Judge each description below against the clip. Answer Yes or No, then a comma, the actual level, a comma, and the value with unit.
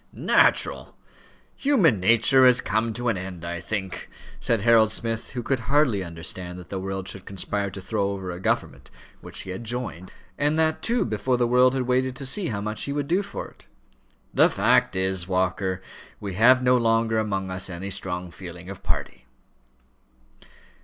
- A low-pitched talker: Yes, low, 105 Hz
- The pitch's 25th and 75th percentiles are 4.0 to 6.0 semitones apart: Yes, average, 5.1 semitones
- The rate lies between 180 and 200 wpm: Yes, average, 185 wpm